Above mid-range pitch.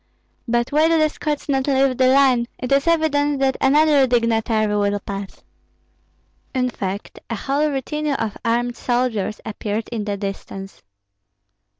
Yes: very high, 250 Hz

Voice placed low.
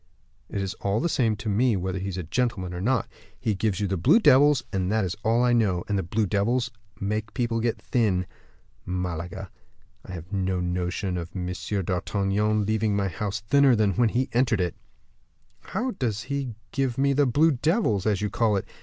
Yes: low, 105 Hz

